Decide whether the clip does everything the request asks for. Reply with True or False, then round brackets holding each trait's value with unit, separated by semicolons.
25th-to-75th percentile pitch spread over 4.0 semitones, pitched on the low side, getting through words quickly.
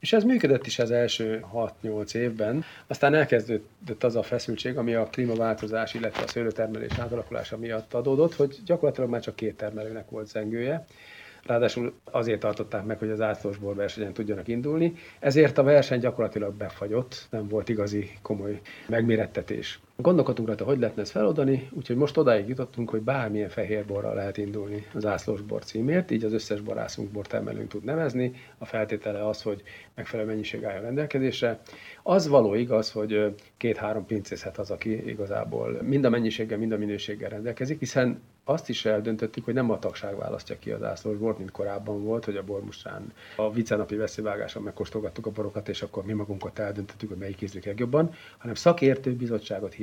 False (2.9 semitones; 110 Hz; 165 wpm)